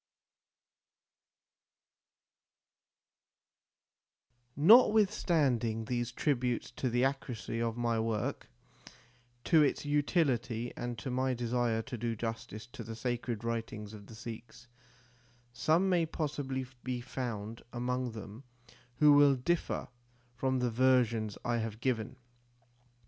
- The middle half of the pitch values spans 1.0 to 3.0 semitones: Yes, average, 2.7 semitones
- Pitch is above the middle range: No, low, 120 Hz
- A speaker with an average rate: No, slow, 110 wpm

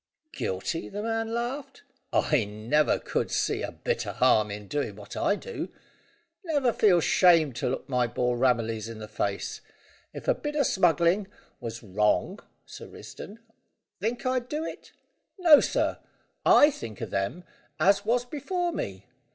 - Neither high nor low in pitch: Yes, medium, 170 Hz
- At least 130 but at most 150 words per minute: No, average, 160 wpm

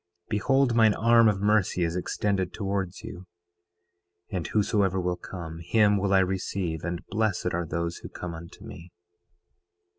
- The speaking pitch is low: Yes, very low, 95 Hz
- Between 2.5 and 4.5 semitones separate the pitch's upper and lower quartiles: Yes, average, 3.1 semitones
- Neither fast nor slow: Yes, average, 150 wpm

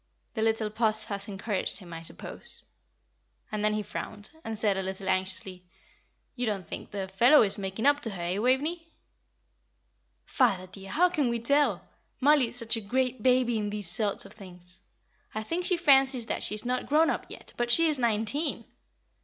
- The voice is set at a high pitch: Yes, high, 220 Hz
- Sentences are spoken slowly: No, average, 190 wpm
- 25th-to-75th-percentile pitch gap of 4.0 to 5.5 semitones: Yes, average, 4.6 semitones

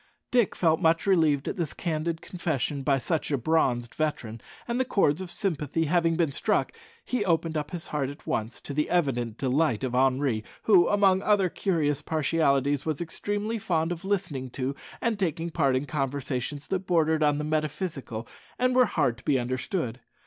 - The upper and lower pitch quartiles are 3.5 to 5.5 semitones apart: Yes, average, 4.4 semitones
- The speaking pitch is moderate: Yes, medium, 155 Hz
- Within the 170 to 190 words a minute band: Yes, average, 180 wpm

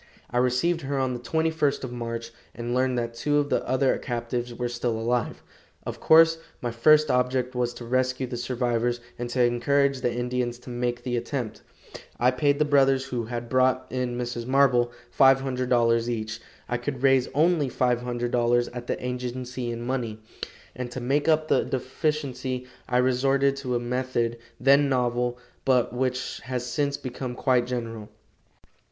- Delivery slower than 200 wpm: Yes, average, 165 wpm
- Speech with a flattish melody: Yes, narrow, 1.7 semitones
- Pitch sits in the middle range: No, low, 125 Hz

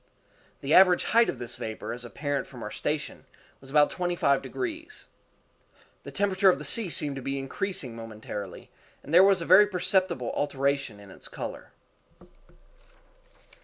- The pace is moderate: Yes, average, 160 wpm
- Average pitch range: No, wide, 6.1 semitones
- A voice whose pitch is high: No, medium, 145 Hz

